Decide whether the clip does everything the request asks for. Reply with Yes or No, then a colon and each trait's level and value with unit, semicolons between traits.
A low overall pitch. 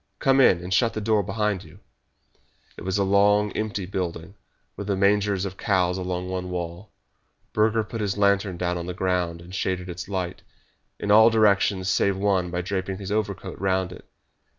Yes: very low, 95 Hz